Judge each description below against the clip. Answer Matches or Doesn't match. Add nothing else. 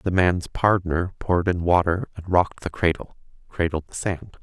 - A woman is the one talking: Doesn't match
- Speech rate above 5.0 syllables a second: Doesn't match